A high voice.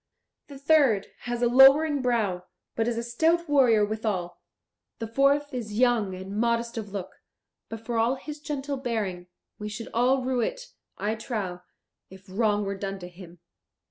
Yes: high, 230 Hz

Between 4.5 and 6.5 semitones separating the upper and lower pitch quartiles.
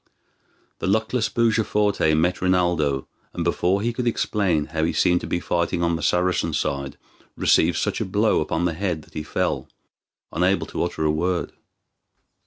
No: average, 3.9 semitones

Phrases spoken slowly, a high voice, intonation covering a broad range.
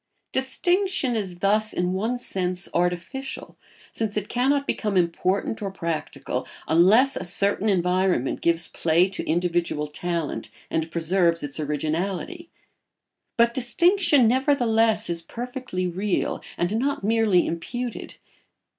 Yes: slow, 120 wpm; high, 195 Hz; wide, 5.8 semitones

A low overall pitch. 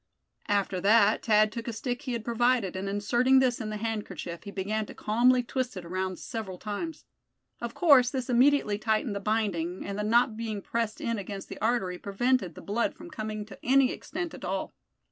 No: high, 220 Hz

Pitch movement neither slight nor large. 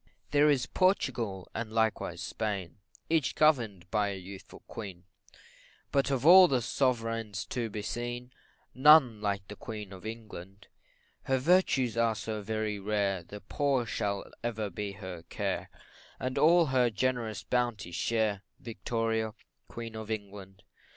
Yes: average, 3.7 semitones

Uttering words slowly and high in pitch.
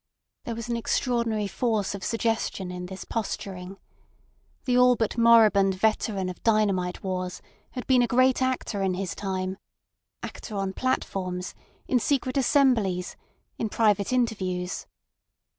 Yes: slow, 130 wpm; high, 210 Hz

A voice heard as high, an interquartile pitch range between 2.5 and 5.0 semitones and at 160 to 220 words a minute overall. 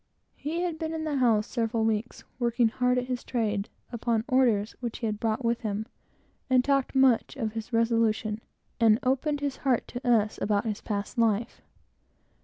Yes: high, 235 Hz; average, 2.9 semitones; average, 180 wpm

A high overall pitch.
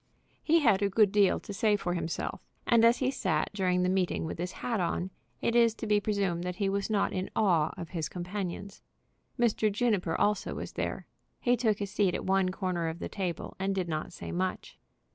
Yes: high, 195 Hz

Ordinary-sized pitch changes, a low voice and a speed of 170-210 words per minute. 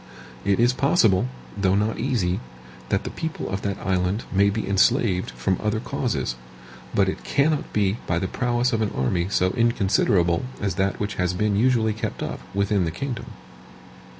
Yes: average, 3.7 semitones; low, 100 Hz; average, 175 wpm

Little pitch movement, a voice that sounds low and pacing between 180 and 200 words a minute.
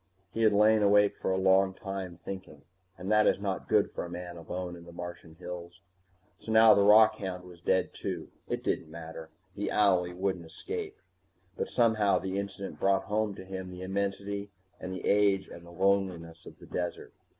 Yes: narrow, 2.3 semitones; very low, 95 Hz; average, 190 wpm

